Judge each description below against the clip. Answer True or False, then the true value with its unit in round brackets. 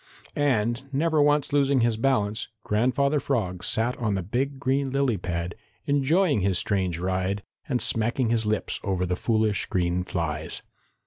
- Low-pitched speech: True (115 Hz)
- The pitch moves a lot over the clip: True (6.5 semitones)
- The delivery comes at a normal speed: True (150 wpm)